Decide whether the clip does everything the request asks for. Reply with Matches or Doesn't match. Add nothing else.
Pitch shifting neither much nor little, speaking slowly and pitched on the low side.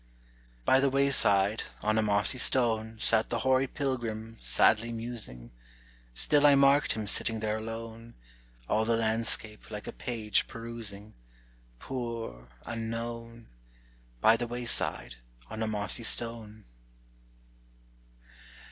Doesn't match